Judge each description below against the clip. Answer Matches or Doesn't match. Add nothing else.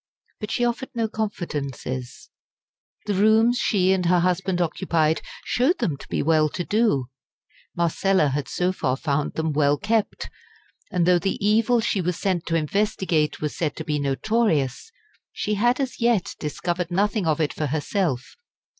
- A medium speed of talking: Matches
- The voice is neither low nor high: Matches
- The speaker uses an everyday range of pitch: Doesn't match